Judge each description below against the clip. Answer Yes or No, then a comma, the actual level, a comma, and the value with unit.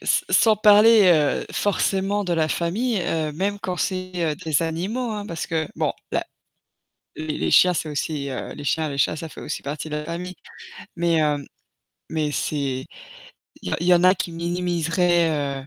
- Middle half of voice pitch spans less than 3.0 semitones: No, average, 3.4 semitones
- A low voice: No, medium, 170 Hz